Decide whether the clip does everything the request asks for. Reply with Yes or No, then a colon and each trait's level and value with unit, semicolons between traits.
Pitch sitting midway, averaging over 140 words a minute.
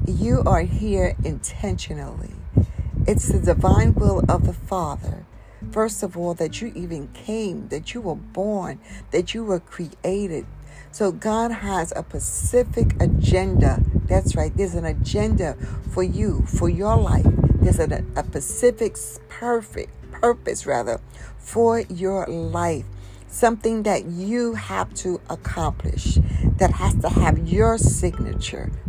No: medium, 145 Hz; slow, 135 wpm